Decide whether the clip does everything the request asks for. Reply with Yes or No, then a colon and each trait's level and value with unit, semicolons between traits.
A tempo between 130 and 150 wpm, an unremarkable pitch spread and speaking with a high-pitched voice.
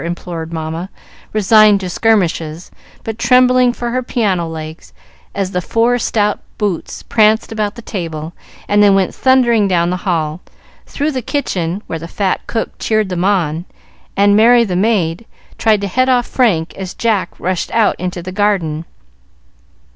No: average, 160 wpm; average, 4.6 semitones; high, 200 Hz